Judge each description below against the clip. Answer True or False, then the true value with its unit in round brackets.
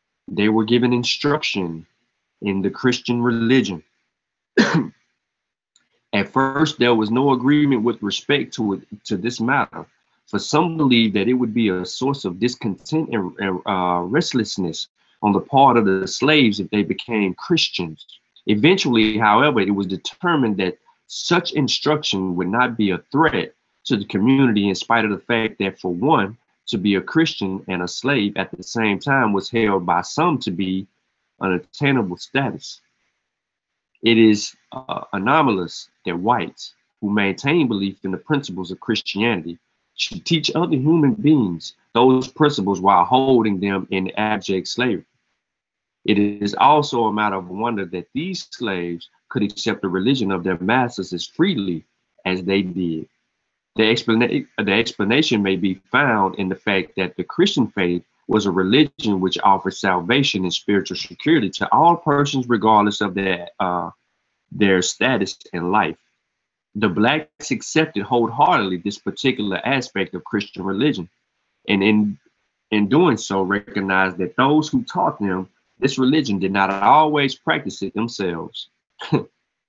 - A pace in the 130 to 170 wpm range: True (150 wpm)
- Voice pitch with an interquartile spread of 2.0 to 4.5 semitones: False (5.1 semitones)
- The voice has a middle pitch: False (105 Hz)